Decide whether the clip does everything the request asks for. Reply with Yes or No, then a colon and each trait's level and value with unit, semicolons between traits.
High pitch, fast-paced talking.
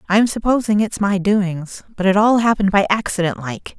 No: high, 200 Hz; average, 190 wpm